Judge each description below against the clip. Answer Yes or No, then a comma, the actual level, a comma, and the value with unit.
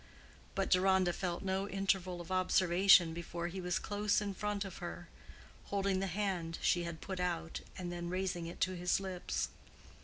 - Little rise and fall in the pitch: Yes, narrow, 1.9 semitones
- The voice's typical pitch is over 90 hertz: Yes, medium, 185 Hz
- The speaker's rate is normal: Yes, average, 175 wpm